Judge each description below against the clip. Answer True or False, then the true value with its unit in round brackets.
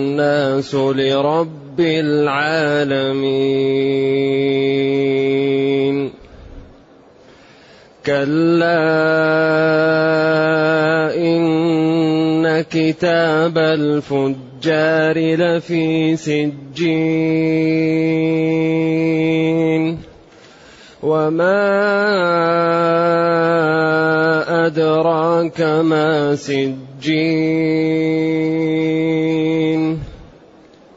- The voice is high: False (160 Hz)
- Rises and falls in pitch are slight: True (1.6 semitones)